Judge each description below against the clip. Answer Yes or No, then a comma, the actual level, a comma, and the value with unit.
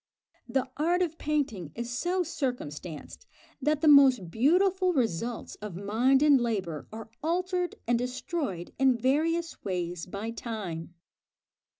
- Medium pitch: No, very high, 250 Hz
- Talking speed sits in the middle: No, slow, 125 wpm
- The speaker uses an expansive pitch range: Yes, wide, 7.2 semitones